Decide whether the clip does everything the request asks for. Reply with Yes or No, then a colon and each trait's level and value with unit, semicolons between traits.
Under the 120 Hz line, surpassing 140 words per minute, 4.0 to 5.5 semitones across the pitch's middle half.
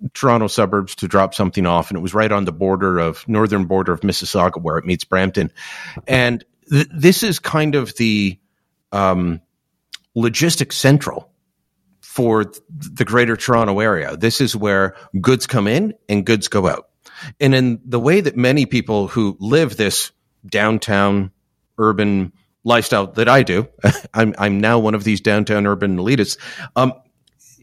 Yes: low, 110 Hz; average, 160 wpm; average, 4.4 semitones